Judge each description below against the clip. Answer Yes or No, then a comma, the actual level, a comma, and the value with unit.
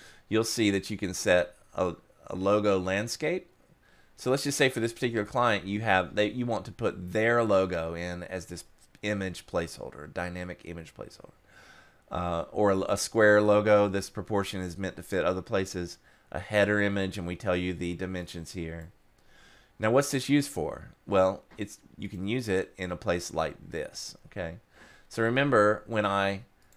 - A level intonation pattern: No, average, 3.4 semitones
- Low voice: Yes, low, 100 Hz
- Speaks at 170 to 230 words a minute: Yes, average, 180 wpm